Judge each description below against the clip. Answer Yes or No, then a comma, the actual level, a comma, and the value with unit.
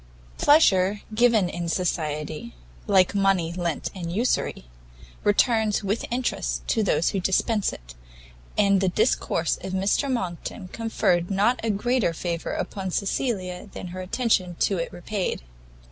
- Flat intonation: No, average, 3.7 semitones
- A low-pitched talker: No, high, 195 Hz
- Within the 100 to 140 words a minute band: Yes, slow, 135 wpm